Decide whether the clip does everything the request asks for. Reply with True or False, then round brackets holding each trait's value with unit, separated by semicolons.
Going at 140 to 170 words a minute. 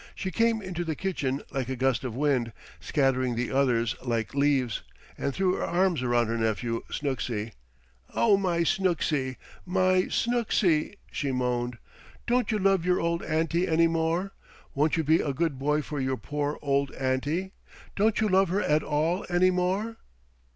True (165 wpm)